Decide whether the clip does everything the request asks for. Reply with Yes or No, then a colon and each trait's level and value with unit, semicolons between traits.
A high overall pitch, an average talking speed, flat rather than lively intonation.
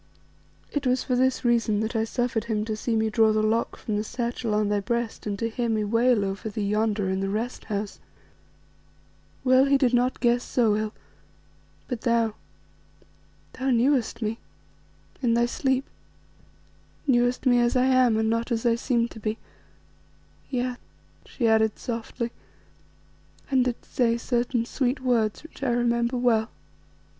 Yes: high, 235 Hz; average, 165 wpm; narrow, 2.2 semitones